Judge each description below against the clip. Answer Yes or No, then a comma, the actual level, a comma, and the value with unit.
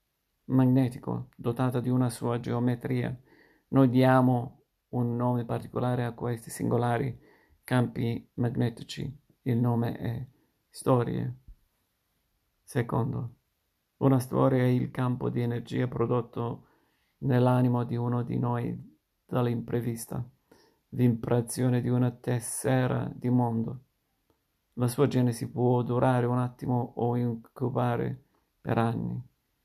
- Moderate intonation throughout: No, narrow, 1.3 semitones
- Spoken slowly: Yes, slow, 105 wpm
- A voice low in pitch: Yes, low, 120 Hz